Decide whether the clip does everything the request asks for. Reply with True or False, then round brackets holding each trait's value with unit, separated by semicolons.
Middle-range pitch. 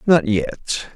False (115 Hz)